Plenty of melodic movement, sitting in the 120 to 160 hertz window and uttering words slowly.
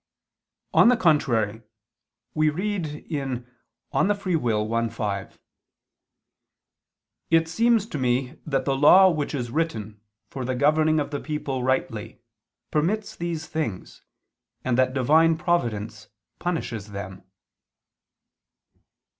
Yes: wide, 5.9 semitones; medium, 140 Hz; slow, 115 wpm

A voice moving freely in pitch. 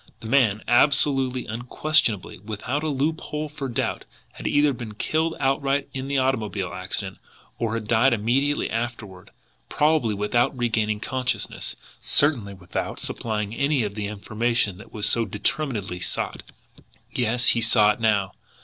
No: average, 4.4 semitones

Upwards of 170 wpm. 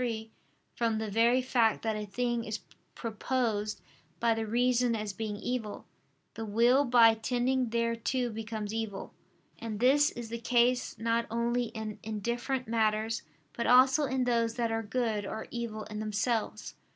No: average, 155 wpm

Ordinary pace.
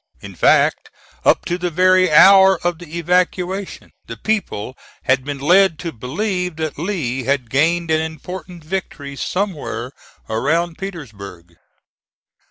No: slow, 130 wpm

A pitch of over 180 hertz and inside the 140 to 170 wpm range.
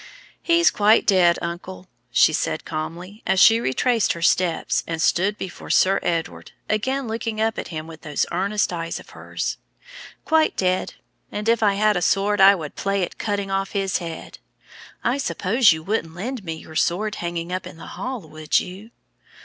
No: high, 190 Hz; average, 180 wpm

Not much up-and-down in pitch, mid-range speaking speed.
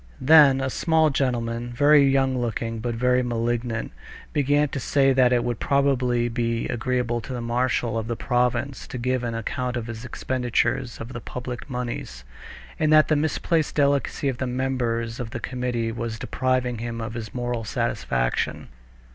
Yes: narrow, 2.1 semitones; average, 170 wpm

